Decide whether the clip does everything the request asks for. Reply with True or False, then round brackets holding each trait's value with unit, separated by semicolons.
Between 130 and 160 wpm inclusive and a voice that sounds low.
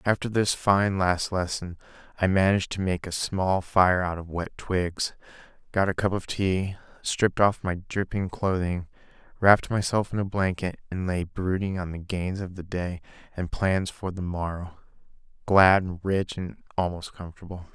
False (170 wpm; 95 Hz)